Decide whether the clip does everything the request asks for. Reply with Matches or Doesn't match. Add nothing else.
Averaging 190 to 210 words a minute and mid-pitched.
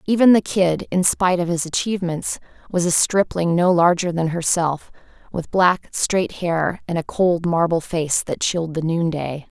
Doesn't match